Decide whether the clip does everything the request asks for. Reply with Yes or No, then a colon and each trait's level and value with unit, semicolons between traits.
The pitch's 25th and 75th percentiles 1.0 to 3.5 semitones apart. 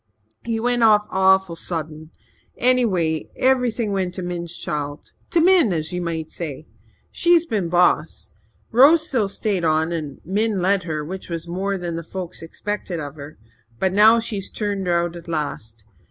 No: average, 4.4 semitones